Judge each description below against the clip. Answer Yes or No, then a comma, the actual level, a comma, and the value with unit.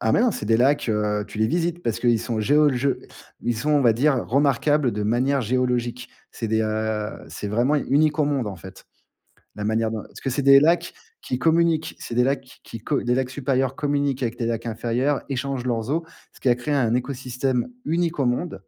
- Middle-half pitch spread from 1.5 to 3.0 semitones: No, average, 3.8 semitones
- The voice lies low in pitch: Yes, low, 125 Hz